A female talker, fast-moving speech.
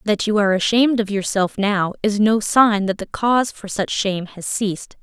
Yes: female; fast, 215 wpm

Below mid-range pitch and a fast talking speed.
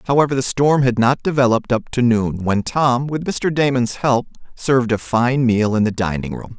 Yes: low, 125 Hz; fast, 210 wpm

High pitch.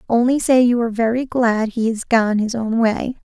Yes: high, 235 Hz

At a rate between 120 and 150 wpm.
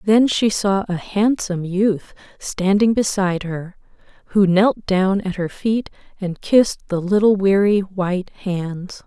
Yes: average, 145 wpm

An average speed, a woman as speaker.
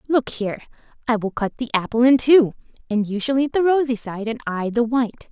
No: fast, 225 wpm; female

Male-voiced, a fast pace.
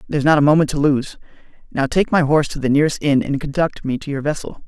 Yes: male; fast, 255 wpm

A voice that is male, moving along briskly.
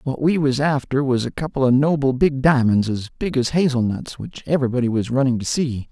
Yes: male; fast, 225 wpm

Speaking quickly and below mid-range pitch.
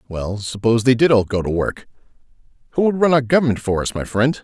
Yes: fast, 230 wpm; low, 120 Hz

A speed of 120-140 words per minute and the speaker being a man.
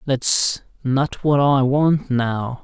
Yes: slow, 135 wpm; male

